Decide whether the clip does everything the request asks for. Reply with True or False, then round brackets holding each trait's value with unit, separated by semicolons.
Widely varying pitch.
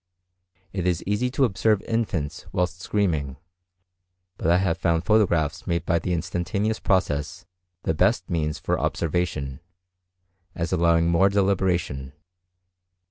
False (3.0 semitones)